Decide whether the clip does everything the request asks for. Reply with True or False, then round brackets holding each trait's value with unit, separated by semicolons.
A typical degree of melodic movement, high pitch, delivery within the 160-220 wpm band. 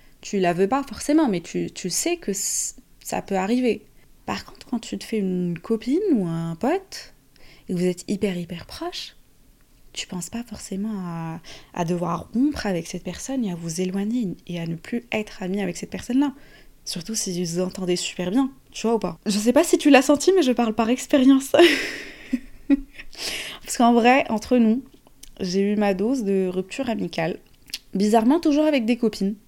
False (6.4 semitones; 215 Hz; 195 wpm)